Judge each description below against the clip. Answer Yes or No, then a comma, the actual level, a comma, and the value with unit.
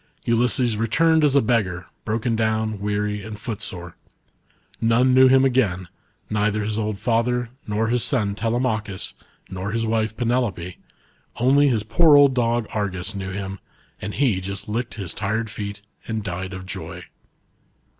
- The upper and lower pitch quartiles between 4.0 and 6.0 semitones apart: No, average, 3.1 semitones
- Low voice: Yes, low, 110 Hz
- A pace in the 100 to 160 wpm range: Yes, average, 150 wpm